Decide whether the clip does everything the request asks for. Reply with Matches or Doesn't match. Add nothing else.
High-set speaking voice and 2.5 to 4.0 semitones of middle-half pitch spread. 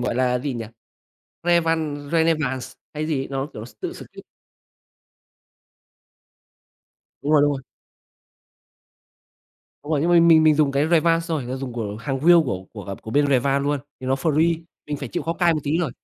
Doesn't match